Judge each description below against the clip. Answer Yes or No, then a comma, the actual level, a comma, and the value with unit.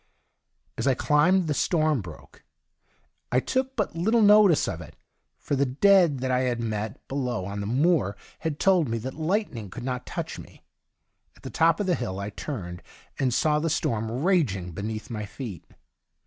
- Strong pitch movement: Yes, wide, 7.4 semitones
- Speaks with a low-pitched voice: Yes, low, 130 Hz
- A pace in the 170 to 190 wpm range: Yes, average, 180 wpm